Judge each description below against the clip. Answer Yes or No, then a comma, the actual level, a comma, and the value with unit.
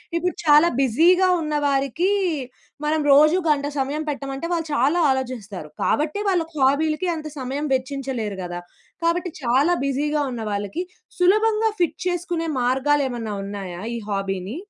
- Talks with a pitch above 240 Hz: Yes, very high, 285 Hz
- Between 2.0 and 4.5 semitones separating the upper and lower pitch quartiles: No, average, 5.2 semitones